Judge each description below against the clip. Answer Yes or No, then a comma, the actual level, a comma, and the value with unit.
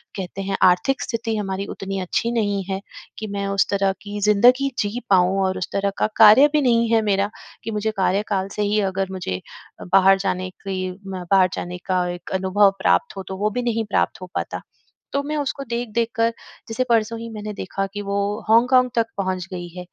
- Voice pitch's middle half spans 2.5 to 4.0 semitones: Yes, average, 3.1 semitones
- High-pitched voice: Yes, high, 200 Hz